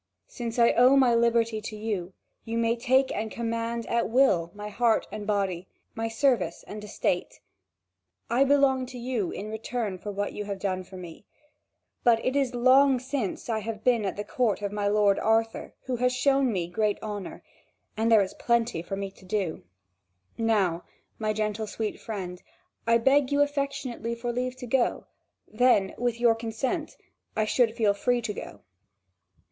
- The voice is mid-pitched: No, high, 225 Hz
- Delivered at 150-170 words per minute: No, average, 180 wpm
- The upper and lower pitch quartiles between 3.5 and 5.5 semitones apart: No, average, 3.1 semitones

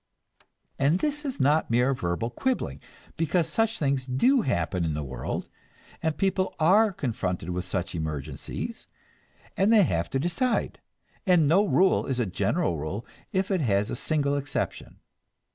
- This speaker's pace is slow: No, average, 155 wpm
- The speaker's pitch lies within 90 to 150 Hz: Yes, medium, 140 Hz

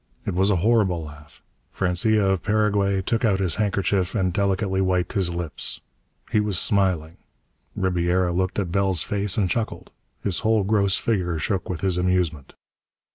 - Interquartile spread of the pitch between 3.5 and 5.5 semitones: No, narrow, 2.4 semitones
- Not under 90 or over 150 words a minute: No, average, 160 wpm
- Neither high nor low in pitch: No, very low, 95 Hz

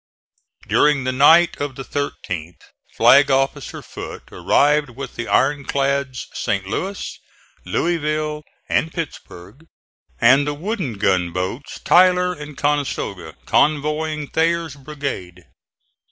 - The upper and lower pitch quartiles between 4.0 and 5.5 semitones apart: No, average, 3.0 semitones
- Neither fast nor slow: No, slow, 110 wpm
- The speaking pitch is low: No, medium, 145 Hz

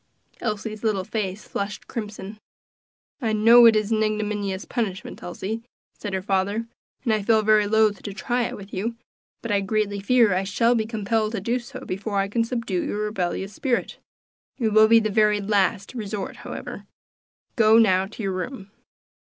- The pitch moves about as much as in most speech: No, narrow, 2.2 semitones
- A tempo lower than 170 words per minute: No, average, 175 wpm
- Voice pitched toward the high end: Yes, high, 215 Hz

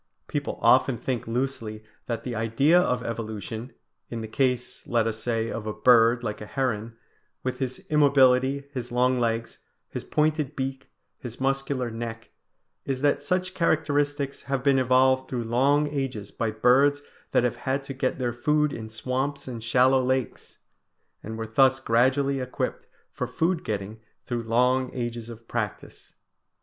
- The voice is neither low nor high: No, low, 125 Hz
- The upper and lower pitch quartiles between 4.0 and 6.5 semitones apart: No, average, 3.0 semitones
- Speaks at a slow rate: No, average, 160 wpm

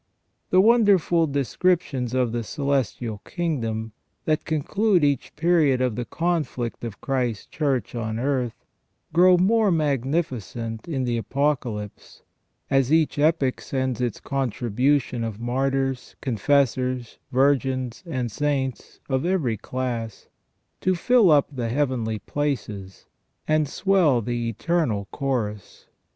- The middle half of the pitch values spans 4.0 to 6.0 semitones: Yes, average, 4.5 semitones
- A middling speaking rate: No, slow, 115 wpm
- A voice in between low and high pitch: No, low, 130 Hz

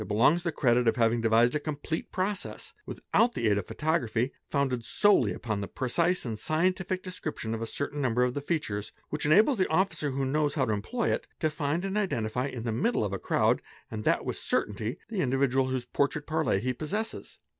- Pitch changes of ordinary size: No, wide, 6.6 semitones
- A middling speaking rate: No, fast, 210 wpm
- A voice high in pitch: No, medium, 140 Hz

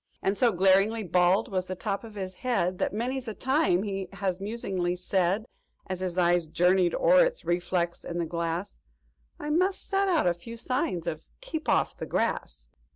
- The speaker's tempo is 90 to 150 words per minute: No, average, 185 wpm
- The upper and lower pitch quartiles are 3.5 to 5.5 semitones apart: Yes, average, 4.8 semitones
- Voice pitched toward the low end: No, high, 190 Hz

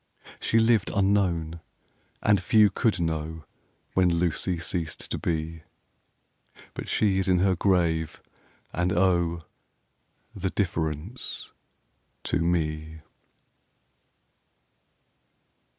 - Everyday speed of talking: No, slow, 95 wpm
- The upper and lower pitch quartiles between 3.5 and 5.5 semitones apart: No, average, 2.9 semitones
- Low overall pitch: Yes, very low, 85 Hz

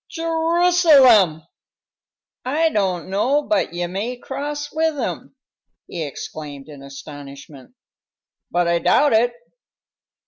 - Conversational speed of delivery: No, slow, 115 wpm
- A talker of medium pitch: No, high, 220 Hz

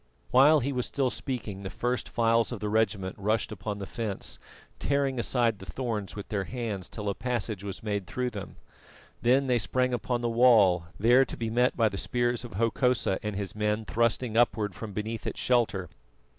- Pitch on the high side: No, low, 115 Hz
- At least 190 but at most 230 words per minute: Yes, average, 195 wpm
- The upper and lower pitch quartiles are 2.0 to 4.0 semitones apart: Yes, average, 3.2 semitones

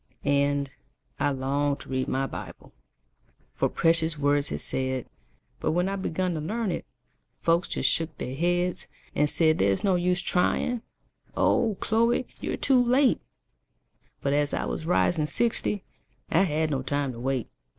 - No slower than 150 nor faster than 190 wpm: Yes, average, 160 wpm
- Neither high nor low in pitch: Yes, medium, 160 Hz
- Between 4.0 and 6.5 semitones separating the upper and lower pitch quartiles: Yes, average, 4.5 semitones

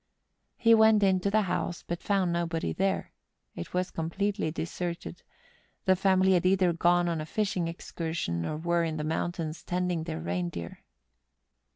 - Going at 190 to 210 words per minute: No, average, 165 wpm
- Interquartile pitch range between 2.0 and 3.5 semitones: Yes, average, 2.7 semitones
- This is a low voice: No, medium, 175 Hz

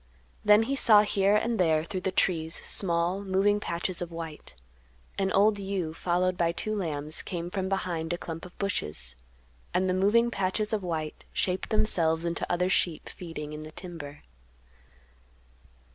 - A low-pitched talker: No, medium, 180 Hz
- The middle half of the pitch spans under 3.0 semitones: No, average, 3.3 semitones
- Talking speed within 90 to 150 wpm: No, average, 160 wpm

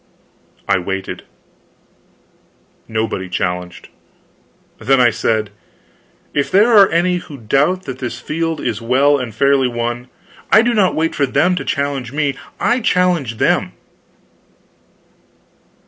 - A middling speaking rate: No, slow, 125 wpm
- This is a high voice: No, low, 135 Hz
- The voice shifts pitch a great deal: Yes, wide, 6.2 semitones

